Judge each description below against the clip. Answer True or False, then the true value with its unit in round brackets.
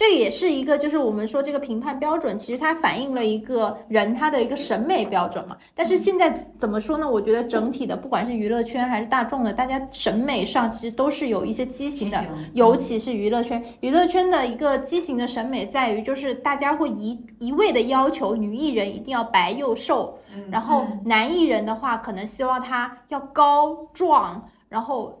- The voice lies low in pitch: False (250 Hz)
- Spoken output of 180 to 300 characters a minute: False (310 characters per minute)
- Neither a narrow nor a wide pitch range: True (4.2 semitones)